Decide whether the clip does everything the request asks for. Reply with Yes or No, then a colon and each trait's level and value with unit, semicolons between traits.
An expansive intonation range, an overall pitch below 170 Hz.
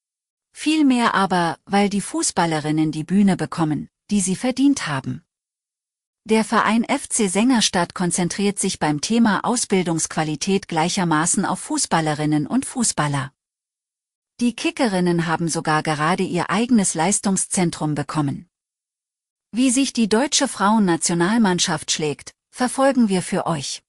No: wide, 5.9 semitones; high, 190 Hz